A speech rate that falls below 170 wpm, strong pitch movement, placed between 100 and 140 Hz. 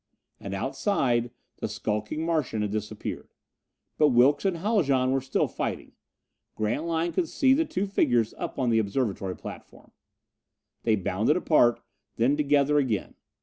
Yes: average, 140 wpm; wide, 6.4 semitones; low, 135 Hz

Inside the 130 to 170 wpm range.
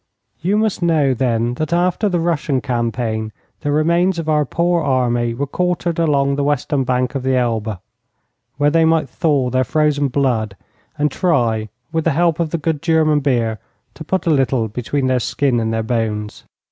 No: average, 185 wpm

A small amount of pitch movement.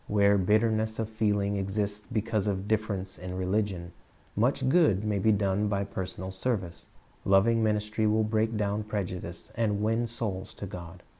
Yes: narrow, 2.2 semitones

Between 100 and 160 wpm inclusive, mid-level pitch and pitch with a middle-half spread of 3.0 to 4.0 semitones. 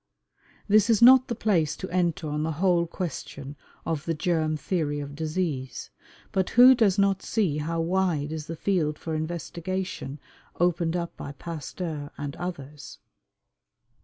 Yes: average, 150 wpm; medium, 165 Hz; average, 3.6 semitones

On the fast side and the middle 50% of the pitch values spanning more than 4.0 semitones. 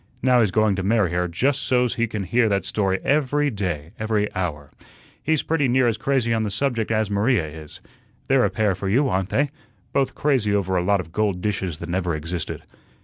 Yes: fast, 210 wpm; average, 5.1 semitones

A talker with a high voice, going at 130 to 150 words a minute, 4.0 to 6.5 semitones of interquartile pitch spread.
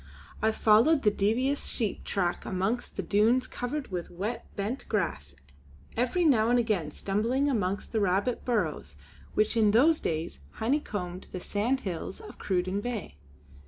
Yes: high, 215 Hz; average, 145 wpm; average, 4.7 semitones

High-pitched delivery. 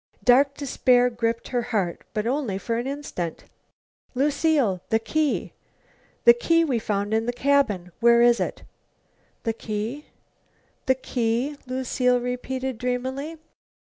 Yes: very high, 250 Hz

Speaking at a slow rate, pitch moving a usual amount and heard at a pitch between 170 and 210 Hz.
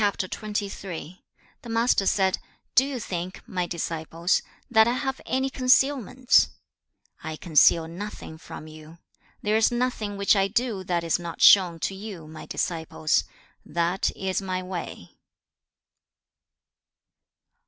Yes: slow, 120 wpm; average, 4.6 semitones; high, 190 Hz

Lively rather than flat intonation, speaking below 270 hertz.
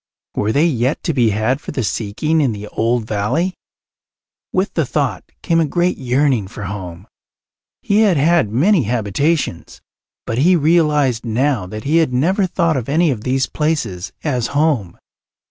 Yes: wide, 6.6 semitones; low, 135 Hz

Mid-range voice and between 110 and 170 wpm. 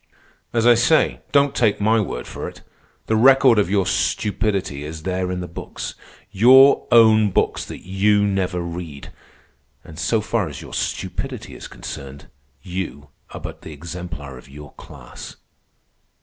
No: very low, 95 Hz; average, 155 wpm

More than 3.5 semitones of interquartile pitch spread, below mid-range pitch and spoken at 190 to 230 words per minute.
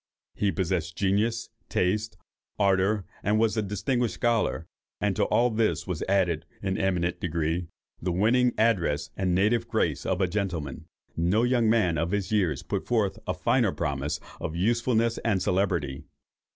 No: average, 4.2 semitones; very low, 95 Hz; average, 155 wpm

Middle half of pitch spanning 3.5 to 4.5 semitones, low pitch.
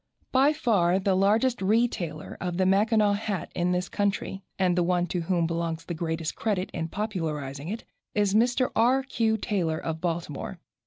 No: average, 4.2 semitones; high, 190 Hz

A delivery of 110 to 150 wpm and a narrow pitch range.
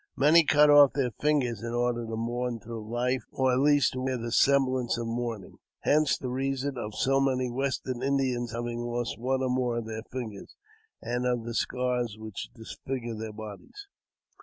No: average, 185 wpm; narrow, 2.2 semitones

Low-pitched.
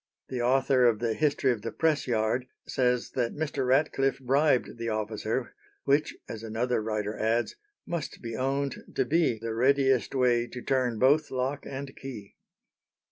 Yes: low, 125 Hz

